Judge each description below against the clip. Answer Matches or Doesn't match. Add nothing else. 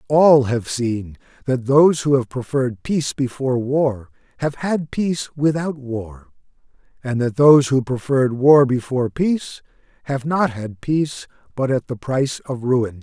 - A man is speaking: Matches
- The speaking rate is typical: Matches